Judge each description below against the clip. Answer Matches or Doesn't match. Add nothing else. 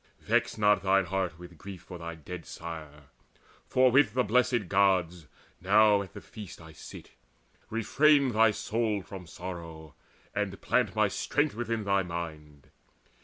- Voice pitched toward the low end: Matches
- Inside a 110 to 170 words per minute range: Matches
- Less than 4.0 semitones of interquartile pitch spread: Doesn't match